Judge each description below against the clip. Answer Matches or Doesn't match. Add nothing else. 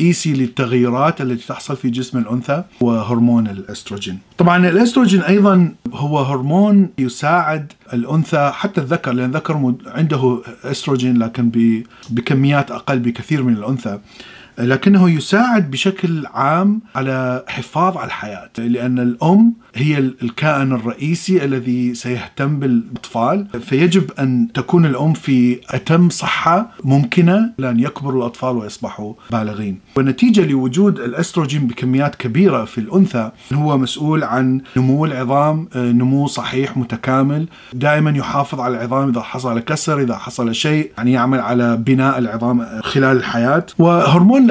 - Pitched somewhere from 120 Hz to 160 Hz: Matches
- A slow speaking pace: Doesn't match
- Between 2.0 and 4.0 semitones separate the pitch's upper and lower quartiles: Doesn't match